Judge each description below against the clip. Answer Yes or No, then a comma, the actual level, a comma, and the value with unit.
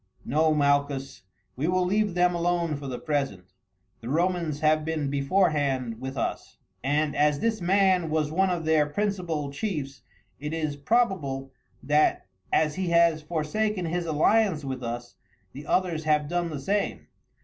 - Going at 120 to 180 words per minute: Yes, average, 155 wpm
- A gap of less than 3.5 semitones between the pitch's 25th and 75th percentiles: No, average, 3.8 semitones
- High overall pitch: No, medium, 155 Hz